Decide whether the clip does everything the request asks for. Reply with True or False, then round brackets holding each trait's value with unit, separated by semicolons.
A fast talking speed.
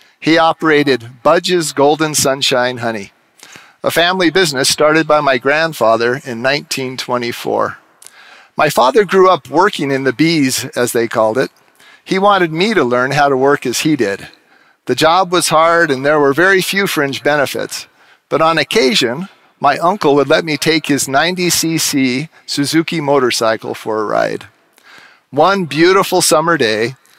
False (150 wpm)